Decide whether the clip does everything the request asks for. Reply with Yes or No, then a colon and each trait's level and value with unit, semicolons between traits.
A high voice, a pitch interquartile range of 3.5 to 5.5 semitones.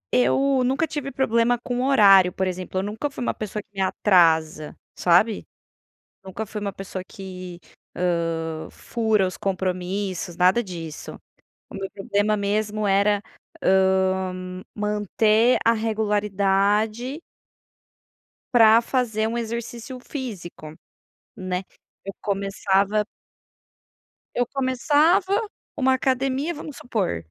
Yes: high, 205 Hz; average, 4.1 semitones